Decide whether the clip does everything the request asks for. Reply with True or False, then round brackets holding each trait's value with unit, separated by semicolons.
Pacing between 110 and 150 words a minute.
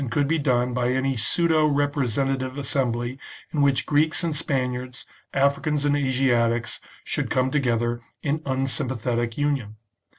True (135 wpm)